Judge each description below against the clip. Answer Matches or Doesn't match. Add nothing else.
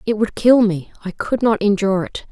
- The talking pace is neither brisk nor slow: Doesn't match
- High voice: Matches